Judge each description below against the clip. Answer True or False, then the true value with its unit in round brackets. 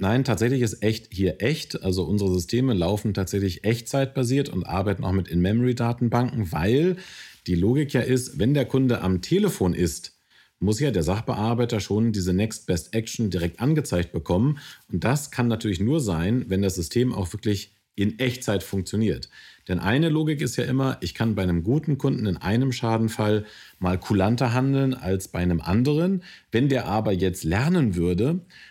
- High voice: False (110 Hz)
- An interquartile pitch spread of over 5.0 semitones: True (5.5 semitones)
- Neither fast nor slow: True (170 wpm)